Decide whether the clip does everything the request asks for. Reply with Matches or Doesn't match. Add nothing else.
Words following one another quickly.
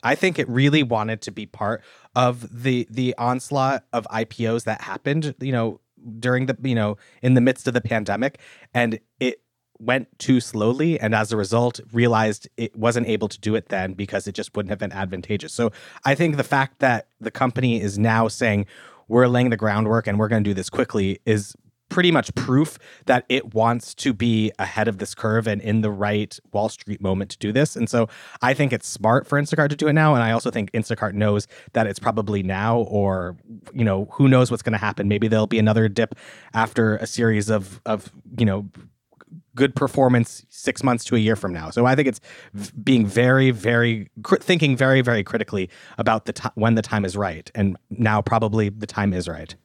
Matches